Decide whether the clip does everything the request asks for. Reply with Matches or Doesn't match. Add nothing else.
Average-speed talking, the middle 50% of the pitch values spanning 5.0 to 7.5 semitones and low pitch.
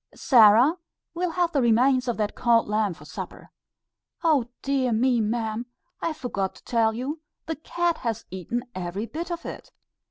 Doesn't match